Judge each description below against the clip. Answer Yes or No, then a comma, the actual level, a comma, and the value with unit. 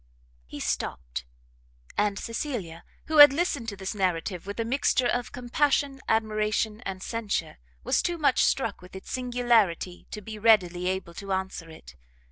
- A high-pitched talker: Yes, high, 210 Hz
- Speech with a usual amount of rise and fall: Yes, average, 4.7 semitones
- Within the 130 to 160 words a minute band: Yes, average, 155 wpm